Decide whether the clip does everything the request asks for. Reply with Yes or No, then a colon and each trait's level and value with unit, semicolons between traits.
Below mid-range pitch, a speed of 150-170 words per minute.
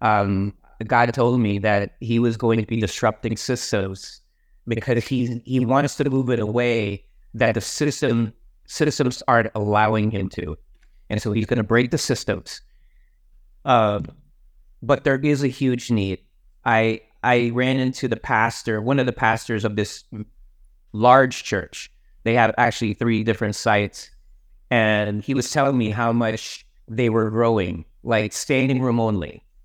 Yes: low, 115 Hz; average, 160 wpm